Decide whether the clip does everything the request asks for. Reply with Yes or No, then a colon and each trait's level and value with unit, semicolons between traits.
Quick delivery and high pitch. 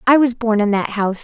Yes: fast, 290 wpm; high, 225 Hz